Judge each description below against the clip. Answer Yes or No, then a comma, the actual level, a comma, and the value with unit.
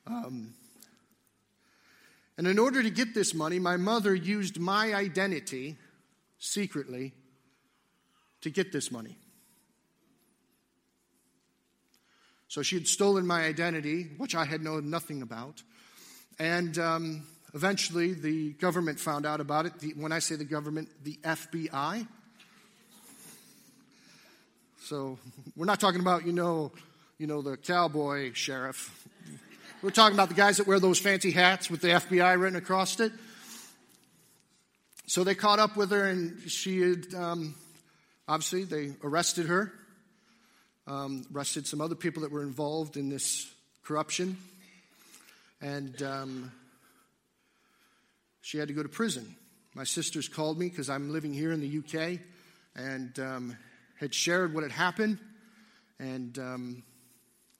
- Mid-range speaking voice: Yes, medium, 165 Hz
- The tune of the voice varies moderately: Yes, average, 4.9 semitones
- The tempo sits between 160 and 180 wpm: No, slow, 135 wpm